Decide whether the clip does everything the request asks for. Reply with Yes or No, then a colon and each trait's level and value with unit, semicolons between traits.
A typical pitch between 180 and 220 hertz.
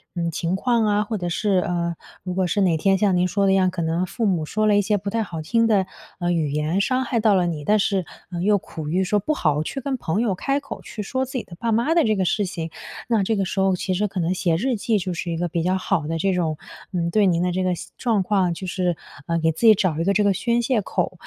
Yes: high, 190 Hz